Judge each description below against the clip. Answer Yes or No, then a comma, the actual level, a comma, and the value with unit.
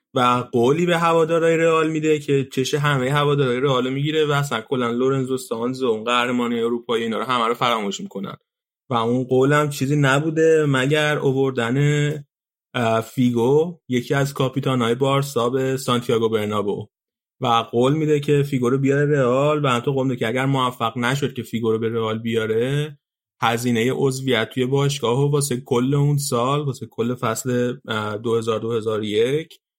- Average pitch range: Yes, average, 3.5 semitones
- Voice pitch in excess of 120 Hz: Yes, low, 130 Hz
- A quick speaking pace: Yes, fast, 160 wpm